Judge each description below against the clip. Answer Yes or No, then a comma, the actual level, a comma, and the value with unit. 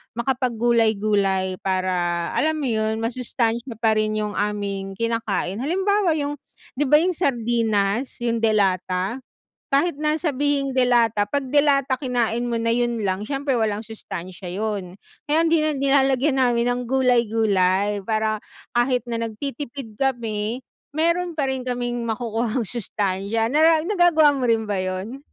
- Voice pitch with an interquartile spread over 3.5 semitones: Yes, average, 4.4 semitones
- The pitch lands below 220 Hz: No, high, 235 Hz